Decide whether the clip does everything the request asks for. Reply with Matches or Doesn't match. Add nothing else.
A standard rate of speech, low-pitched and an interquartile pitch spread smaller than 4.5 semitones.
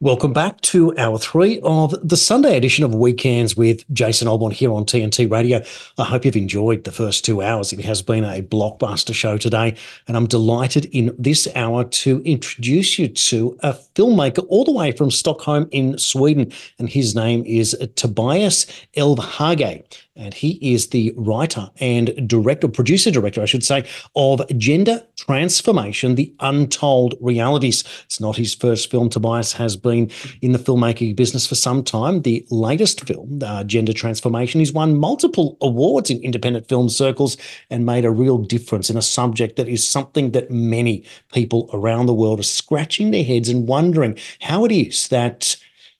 Matches